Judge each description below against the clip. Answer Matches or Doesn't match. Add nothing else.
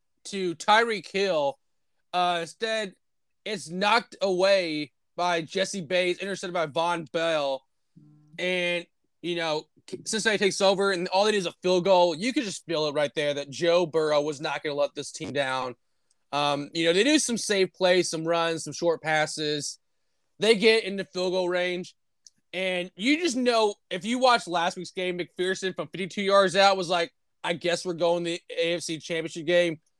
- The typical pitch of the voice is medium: Matches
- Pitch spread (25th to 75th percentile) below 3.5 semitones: Matches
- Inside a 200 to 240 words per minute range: Doesn't match